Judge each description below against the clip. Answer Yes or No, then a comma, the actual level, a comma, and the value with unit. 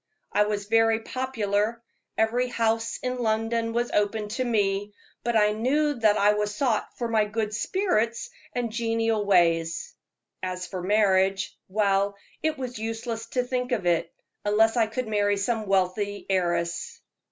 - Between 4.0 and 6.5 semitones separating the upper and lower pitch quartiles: No, narrow, 2.5 semitones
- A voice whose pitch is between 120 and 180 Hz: No, high, 220 Hz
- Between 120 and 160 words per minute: Yes, average, 150 wpm